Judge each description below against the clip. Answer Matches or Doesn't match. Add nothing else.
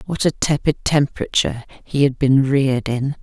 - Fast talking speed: Doesn't match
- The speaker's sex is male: Doesn't match